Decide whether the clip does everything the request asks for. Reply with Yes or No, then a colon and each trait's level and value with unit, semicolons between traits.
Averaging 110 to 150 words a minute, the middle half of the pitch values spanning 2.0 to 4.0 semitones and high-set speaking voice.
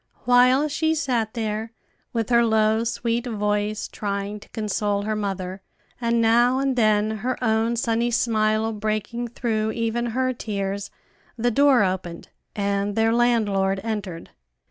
Yes: average, 140 wpm; narrow, 2.4 semitones; high, 220 Hz